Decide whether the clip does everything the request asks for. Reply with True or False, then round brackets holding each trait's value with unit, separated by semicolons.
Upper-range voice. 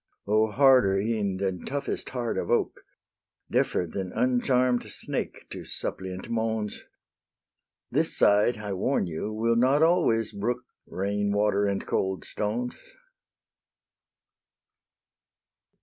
False (110 Hz)